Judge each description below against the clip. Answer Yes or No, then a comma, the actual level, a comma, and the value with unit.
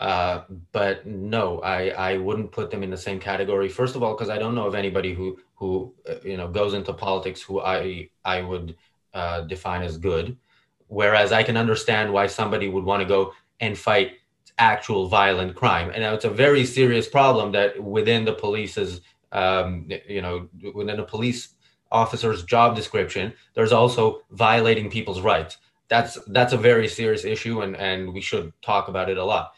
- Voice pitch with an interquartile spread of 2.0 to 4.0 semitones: Yes, average, 3.1 semitones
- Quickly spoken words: No, average, 185 wpm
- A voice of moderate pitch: No, low, 100 Hz